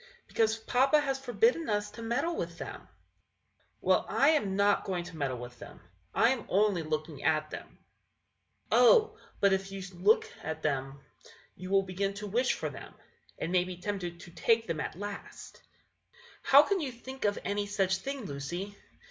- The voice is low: No, high, 200 Hz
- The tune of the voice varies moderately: No, wide, 5.7 semitones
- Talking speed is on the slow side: No, average, 190 wpm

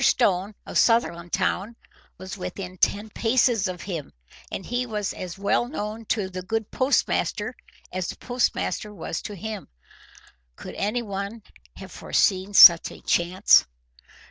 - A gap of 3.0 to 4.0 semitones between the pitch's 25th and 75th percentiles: Yes, average, 3.4 semitones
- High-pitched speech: Yes, high, 200 Hz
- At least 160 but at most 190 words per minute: No, slow, 135 wpm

